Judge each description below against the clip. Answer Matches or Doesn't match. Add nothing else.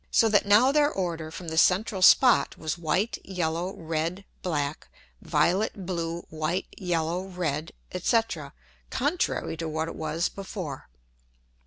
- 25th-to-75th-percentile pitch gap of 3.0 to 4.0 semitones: Matches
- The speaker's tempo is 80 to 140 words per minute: Matches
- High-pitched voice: Doesn't match